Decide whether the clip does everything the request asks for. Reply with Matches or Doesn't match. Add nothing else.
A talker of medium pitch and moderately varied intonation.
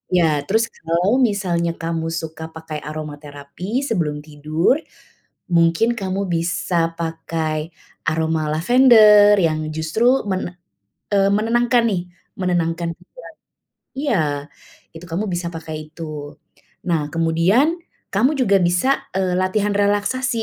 Matches